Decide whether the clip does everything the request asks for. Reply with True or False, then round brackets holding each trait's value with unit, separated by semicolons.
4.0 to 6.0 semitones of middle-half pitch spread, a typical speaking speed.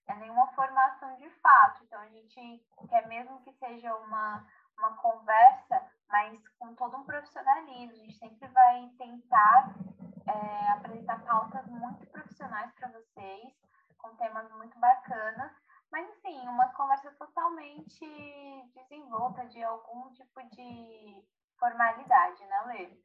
True (4.5 semitones; 130 wpm)